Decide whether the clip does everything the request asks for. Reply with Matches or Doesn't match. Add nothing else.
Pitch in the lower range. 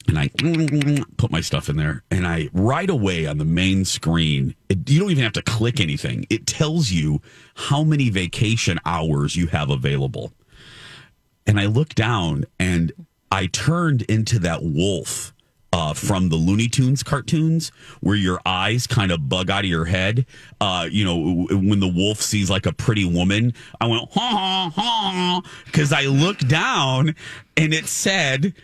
Matches